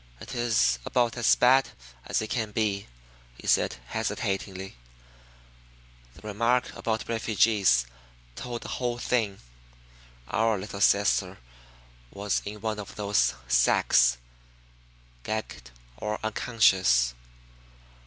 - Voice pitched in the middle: No, low, 105 Hz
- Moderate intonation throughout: Yes, average, 3.1 semitones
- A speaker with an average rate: No, slow, 105 wpm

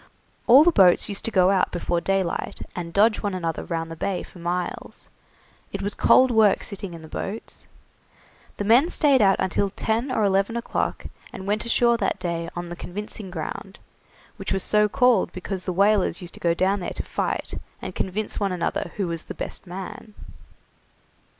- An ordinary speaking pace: Yes, average, 190 wpm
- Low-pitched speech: No, high, 195 Hz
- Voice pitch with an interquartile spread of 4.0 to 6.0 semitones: No, average, 3.2 semitones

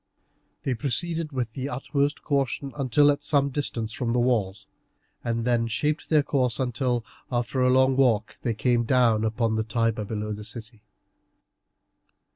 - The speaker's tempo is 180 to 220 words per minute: No, average, 155 wpm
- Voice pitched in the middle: No, low, 125 Hz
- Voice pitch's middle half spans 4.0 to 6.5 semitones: No, average, 3.4 semitones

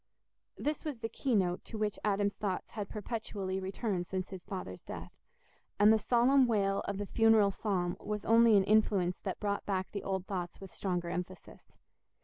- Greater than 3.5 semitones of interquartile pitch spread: No, average, 2.7 semitones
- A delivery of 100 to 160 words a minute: No, average, 180 wpm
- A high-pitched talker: Yes, high, 200 Hz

